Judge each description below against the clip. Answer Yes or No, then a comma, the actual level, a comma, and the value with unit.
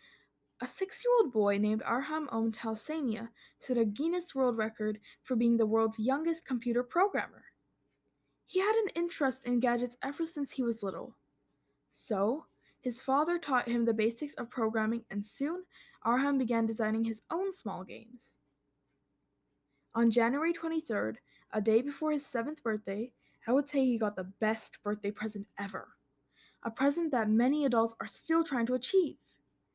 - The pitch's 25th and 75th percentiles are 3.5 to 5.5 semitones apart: Yes, average, 4.9 semitones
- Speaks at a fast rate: No, average, 155 wpm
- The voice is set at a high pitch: Yes, high, 245 Hz